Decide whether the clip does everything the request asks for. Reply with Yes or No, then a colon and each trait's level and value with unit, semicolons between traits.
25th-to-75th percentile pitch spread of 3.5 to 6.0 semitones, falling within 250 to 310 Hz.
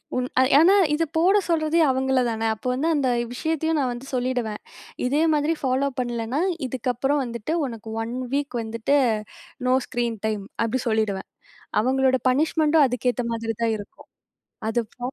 Yes: average, 4.0 semitones; very high, 255 Hz